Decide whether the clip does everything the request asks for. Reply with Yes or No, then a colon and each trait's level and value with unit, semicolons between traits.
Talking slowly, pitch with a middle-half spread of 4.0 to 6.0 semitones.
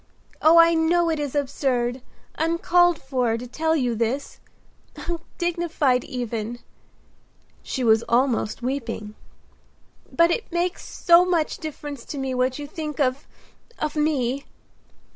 Yes: slow, 125 wpm; average, 5.0 semitones